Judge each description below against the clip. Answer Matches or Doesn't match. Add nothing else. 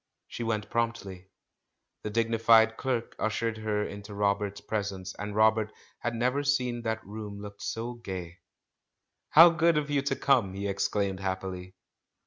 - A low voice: Matches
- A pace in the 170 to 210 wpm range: Doesn't match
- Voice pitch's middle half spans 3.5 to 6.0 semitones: Doesn't match